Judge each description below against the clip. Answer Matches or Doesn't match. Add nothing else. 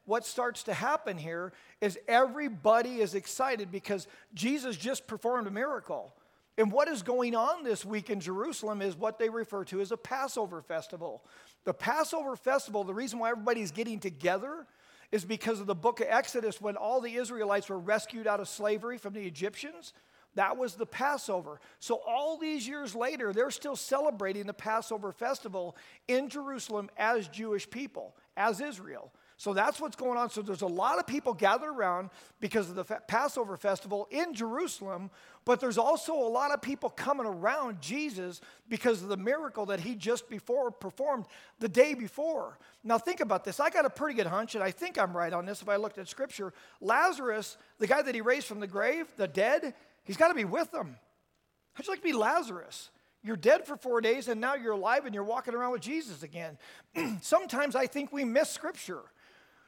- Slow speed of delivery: Doesn't match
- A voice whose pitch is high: Matches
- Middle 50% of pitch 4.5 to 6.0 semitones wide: Matches